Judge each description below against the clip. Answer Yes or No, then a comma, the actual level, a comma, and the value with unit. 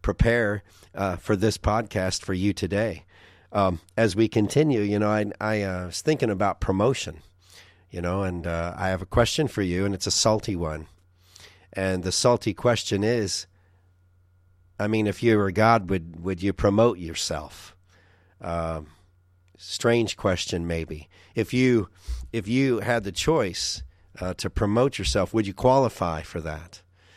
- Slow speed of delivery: No, average, 160 wpm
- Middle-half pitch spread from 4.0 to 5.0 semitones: No, average, 3.3 semitones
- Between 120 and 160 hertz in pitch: No, very low, 95 Hz